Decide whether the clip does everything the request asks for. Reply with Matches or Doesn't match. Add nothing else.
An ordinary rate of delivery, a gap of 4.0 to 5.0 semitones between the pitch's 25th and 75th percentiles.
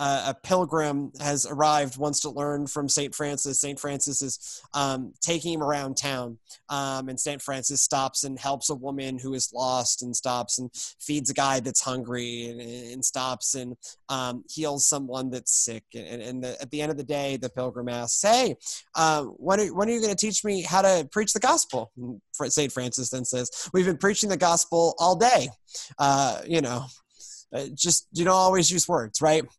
Doesn't match